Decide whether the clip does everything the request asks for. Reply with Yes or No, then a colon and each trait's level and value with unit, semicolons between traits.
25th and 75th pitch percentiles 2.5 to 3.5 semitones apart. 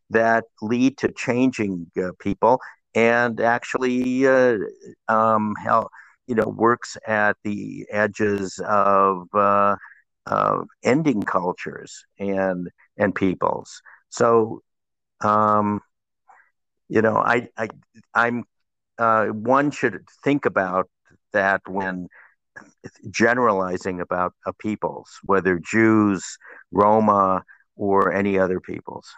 Yes: average, 3.0 semitones